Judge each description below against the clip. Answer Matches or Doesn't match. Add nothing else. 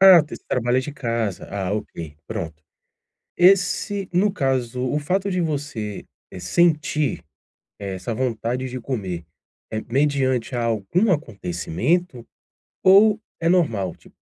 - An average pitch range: Doesn't match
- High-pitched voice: Doesn't match